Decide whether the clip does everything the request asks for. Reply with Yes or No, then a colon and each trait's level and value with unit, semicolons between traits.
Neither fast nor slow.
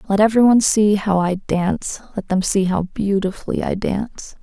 Yes: average, 190 wpm